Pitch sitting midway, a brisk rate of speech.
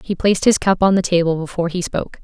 Yes: medium, 180 Hz; fast, 270 wpm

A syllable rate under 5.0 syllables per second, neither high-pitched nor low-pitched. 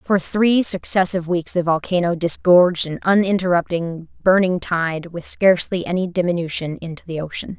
No: 5.1 syllables/s; medium, 175 Hz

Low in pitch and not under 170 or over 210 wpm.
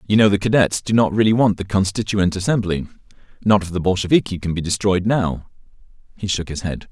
Yes: very low, 95 Hz; average, 190 wpm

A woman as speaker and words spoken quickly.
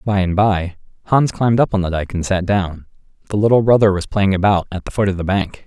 No: male; fast, 255 wpm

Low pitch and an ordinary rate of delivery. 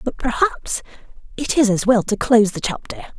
No: high, 240 Hz; average, 190 wpm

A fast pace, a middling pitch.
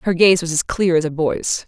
Yes: fast, 285 wpm; medium, 170 Hz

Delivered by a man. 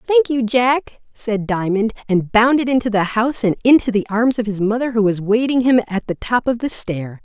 No: female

